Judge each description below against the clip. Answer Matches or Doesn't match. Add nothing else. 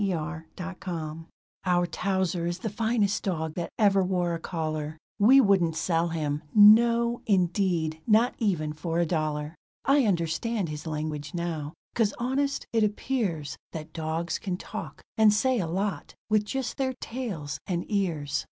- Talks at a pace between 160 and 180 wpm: Doesn't match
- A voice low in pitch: Doesn't match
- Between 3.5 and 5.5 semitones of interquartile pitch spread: Matches